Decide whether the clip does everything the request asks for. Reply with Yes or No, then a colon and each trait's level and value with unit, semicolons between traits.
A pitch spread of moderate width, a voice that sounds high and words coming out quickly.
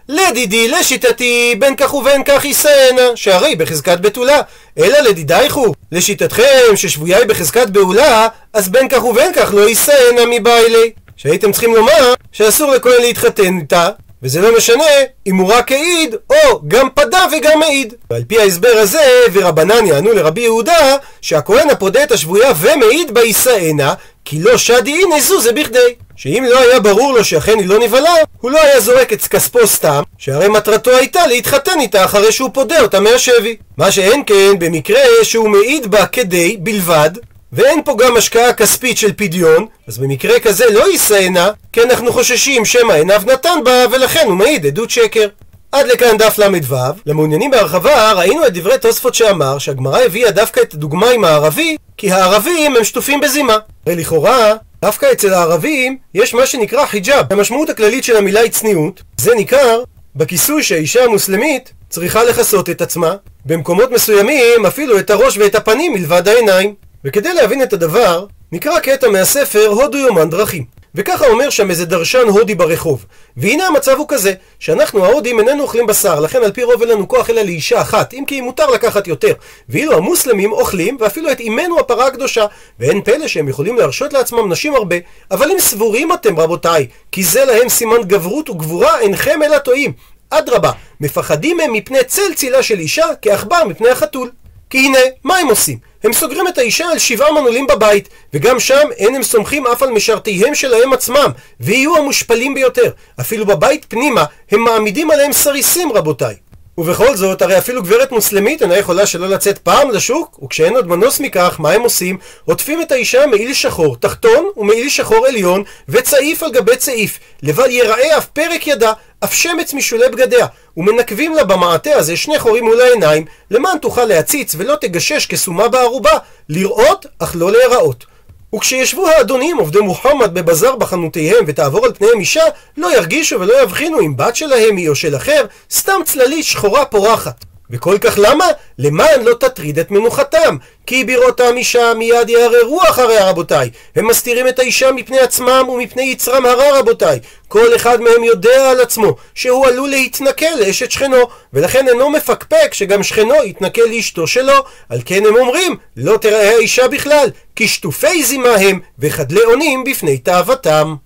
No: wide, 8.1 semitones; very high, 255 Hz; fast, 165 wpm